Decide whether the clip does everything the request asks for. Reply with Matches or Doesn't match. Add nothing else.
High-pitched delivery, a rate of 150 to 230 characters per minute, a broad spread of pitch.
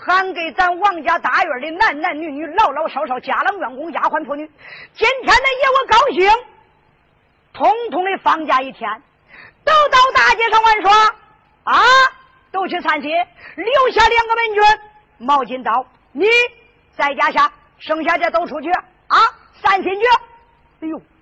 Matches